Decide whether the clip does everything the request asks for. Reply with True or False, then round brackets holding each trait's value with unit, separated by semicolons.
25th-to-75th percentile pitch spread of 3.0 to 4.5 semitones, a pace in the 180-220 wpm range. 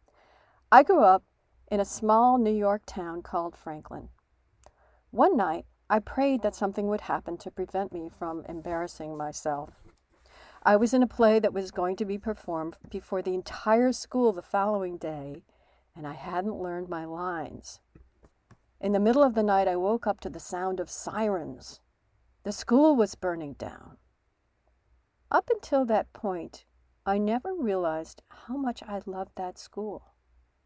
False (4.1 semitones; 160 wpm)